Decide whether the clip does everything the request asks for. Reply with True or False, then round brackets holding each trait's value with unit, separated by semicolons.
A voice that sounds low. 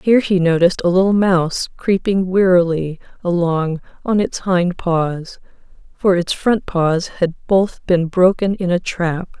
False (180 Hz)